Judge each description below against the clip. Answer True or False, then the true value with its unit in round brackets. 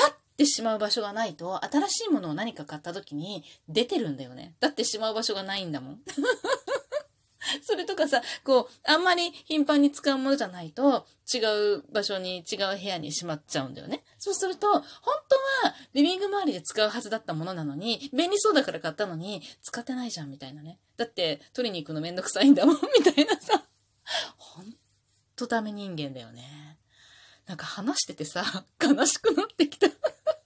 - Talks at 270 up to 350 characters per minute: False (375 characters per minute)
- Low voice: False (230 Hz)